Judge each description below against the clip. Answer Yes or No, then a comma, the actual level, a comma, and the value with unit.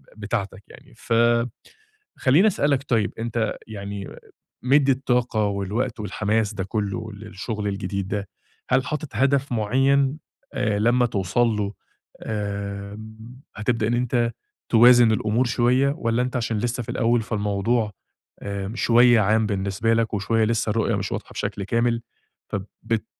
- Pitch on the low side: Yes, low, 115 Hz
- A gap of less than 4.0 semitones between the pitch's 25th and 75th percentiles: Yes, average, 3.0 semitones